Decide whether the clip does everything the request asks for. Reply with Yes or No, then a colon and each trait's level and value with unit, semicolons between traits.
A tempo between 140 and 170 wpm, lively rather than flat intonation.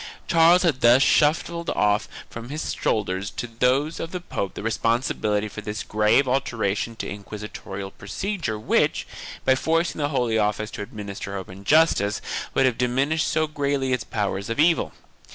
Yes: average, 165 wpm; wide, 6.1 semitones